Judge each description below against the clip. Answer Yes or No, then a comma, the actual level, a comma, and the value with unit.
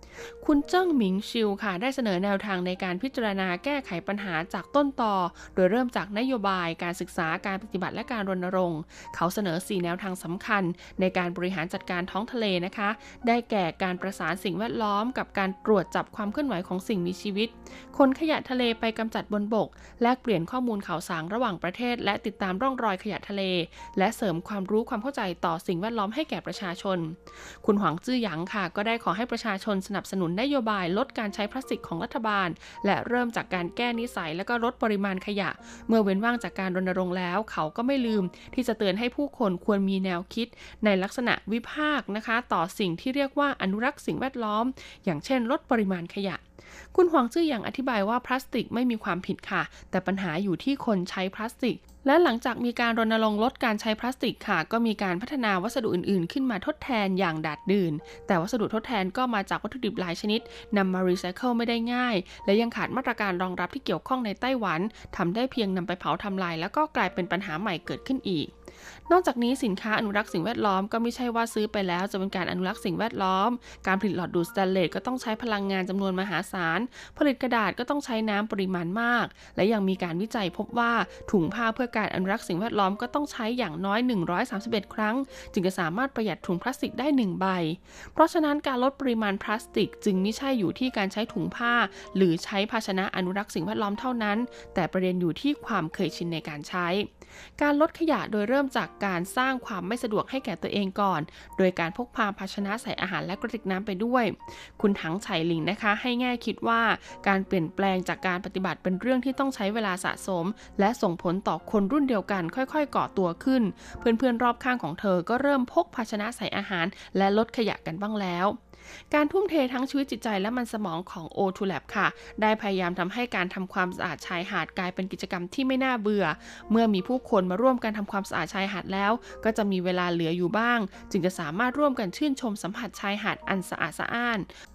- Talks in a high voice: Yes, high, 205 Hz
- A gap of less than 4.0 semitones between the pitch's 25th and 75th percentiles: No, average, 4.3 semitones